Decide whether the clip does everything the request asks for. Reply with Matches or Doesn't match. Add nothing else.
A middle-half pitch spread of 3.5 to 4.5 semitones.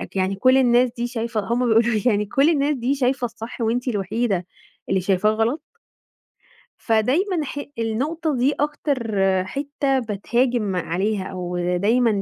Matches